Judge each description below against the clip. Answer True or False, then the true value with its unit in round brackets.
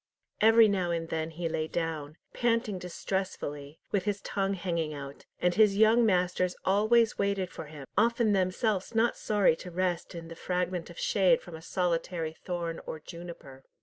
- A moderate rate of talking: True (170 wpm)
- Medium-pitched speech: True (180 Hz)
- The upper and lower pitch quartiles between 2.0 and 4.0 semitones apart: True (3.5 semitones)